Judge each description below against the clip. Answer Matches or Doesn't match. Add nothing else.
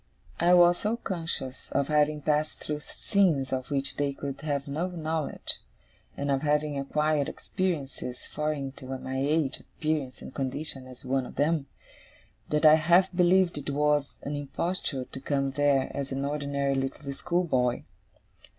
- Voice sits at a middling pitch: Matches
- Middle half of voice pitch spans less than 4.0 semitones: Matches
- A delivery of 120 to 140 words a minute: Doesn't match